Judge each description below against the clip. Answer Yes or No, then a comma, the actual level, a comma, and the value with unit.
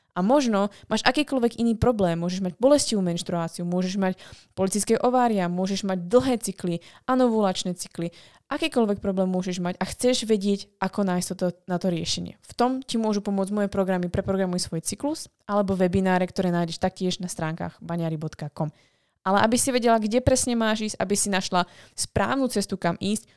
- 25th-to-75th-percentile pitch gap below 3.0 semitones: No, average, 3.7 semitones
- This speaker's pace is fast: Yes, fast, 170 wpm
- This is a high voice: Yes, high, 195 Hz